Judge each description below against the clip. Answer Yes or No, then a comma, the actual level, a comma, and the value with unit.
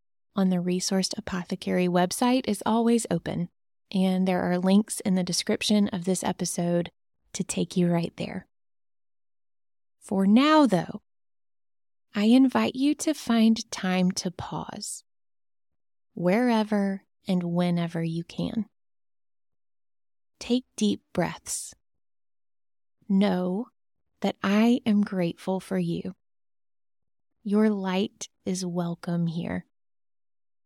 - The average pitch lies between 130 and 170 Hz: No, medium, 180 Hz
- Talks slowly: Yes, slow, 105 wpm